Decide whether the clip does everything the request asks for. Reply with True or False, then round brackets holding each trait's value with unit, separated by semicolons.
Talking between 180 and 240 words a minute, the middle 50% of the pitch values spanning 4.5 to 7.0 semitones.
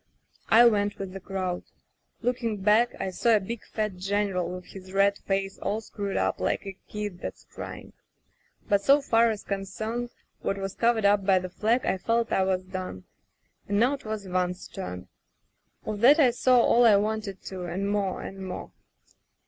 False (185 wpm; 2.8 semitones)